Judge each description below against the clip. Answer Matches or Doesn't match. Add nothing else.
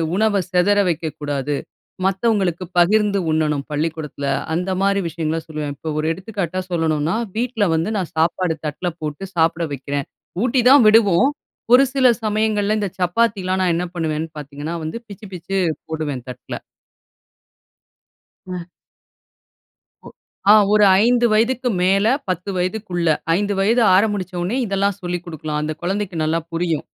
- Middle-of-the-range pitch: Matches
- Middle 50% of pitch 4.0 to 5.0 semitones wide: Matches